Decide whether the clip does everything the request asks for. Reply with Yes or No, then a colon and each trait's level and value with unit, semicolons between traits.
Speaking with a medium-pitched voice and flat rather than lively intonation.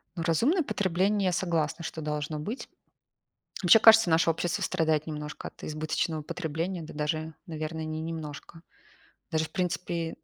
Yes: medium, 160 Hz; narrow, 2.3 semitones